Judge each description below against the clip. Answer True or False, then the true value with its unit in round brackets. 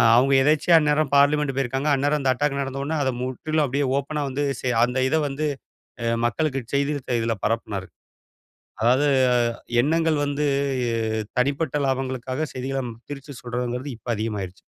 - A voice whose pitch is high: False (135 Hz)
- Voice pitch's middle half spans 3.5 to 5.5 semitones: False (2.9 semitones)